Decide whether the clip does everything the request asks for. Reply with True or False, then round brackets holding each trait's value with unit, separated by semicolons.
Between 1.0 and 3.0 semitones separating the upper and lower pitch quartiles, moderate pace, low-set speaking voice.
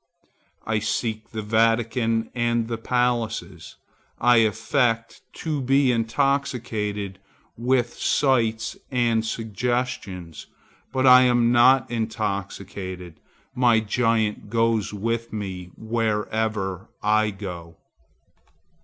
False (2.4 semitones; 90 wpm; 115 Hz)